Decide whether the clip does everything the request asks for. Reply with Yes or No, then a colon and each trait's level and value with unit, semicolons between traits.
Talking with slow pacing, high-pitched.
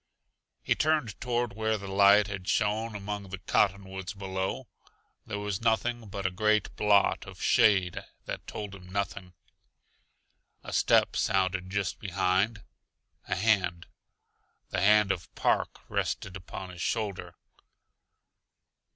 No: slow, 125 wpm; low, 100 Hz